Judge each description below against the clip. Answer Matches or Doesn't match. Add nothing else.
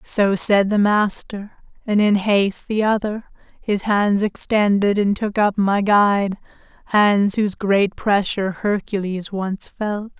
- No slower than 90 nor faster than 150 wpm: Matches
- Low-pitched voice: Doesn't match